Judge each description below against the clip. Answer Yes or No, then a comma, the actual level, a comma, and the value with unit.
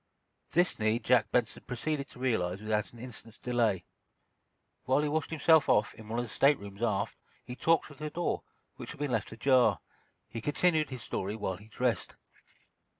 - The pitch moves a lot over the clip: No, average, 5.0 semitones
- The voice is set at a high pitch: No, low, 125 Hz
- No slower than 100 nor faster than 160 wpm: No, average, 180 wpm